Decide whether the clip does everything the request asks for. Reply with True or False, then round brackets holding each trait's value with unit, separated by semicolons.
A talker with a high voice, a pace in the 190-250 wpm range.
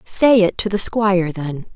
True (195 Hz; 205 wpm)